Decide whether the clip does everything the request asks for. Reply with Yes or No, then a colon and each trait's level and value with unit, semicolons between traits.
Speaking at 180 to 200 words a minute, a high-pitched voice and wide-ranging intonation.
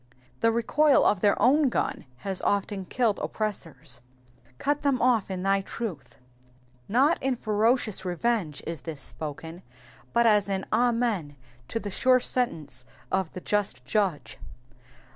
No: average, 140 wpm; high, 205 Hz; wide, 5.9 semitones